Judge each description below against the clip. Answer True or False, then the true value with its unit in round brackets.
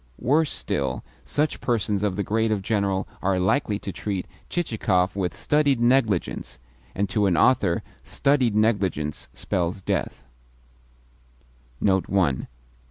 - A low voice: True (100 Hz)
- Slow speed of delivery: True (115 wpm)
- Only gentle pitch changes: False (4.2 semitones)